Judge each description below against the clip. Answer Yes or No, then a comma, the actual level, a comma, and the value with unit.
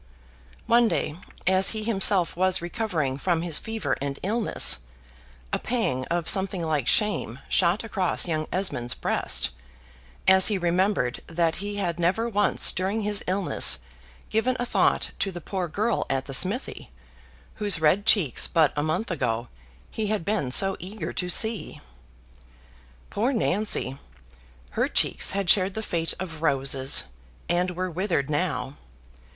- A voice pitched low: No, medium, 185 Hz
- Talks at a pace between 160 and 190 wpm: No, average, 145 wpm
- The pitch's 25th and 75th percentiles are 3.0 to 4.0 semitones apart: No, average, 4.7 semitones